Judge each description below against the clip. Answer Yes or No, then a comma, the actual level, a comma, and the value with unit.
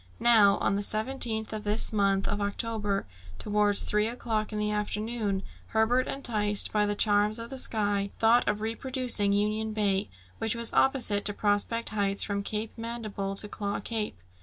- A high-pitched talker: Yes, high, 210 Hz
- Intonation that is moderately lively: No, narrow, 1.8 semitones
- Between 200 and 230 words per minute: No, average, 165 wpm